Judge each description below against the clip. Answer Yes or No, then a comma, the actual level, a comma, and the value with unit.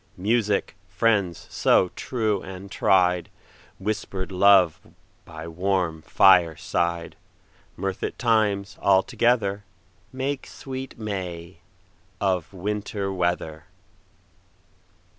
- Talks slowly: Yes, slow, 80 wpm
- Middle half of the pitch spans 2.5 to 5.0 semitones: Yes, average, 2.8 semitones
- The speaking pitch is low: Yes, very low, 95 Hz